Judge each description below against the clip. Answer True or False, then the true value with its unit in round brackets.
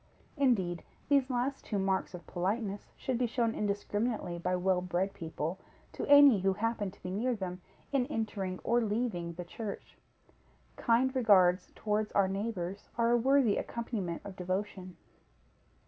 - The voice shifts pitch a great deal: False (4.3 semitones)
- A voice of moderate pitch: False (205 Hz)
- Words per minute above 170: False (150 wpm)